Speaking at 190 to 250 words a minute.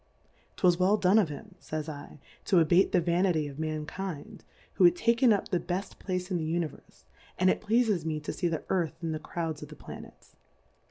Yes: fast, 205 wpm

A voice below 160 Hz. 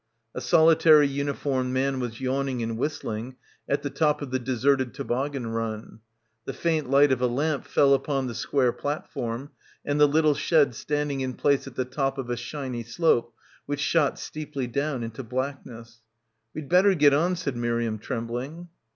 Yes: low, 135 Hz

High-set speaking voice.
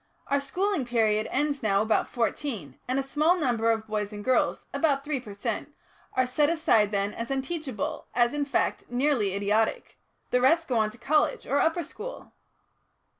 Yes: very high, 255 Hz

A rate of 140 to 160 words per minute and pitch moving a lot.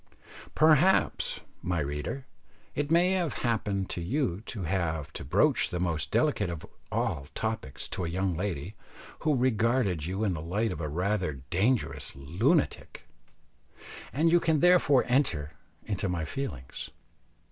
Yes: average, 145 wpm; wide, 8.1 semitones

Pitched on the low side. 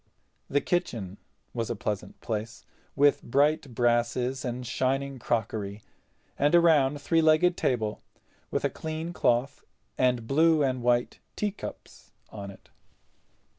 Yes: low, 130 Hz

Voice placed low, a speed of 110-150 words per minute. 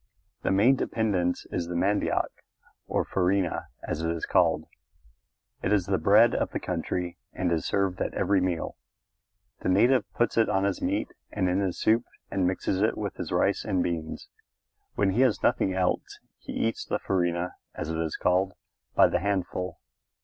No: very low, 95 Hz; average, 180 wpm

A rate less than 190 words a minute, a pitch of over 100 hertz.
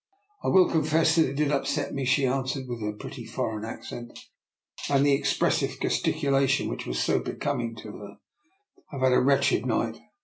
No: average, 195 wpm; low, 135 Hz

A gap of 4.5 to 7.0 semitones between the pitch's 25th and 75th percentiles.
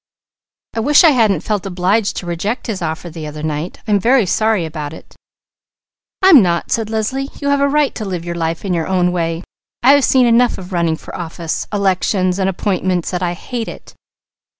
Yes: average, 4.8 semitones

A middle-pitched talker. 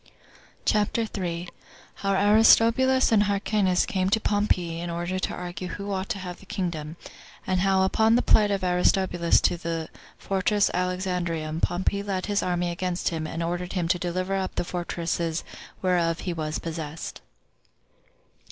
Yes: medium, 180 Hz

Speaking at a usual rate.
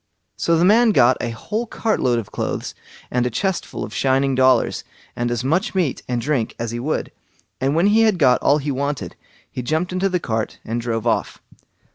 No: fast, 210 wpm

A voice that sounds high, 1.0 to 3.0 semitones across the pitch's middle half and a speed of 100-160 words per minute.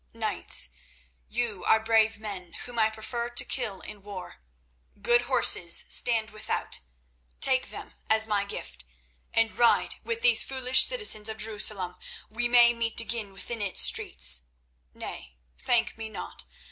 Yes: high, 220 Hz; average, 2.7 semitones; average, 145 wpm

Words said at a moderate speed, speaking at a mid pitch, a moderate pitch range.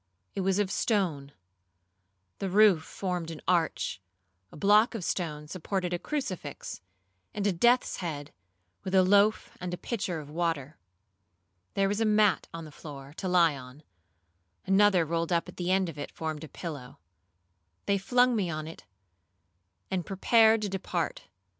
Yes: average, 160 wpm; medium, 180 Hz; average, 4.1 semitones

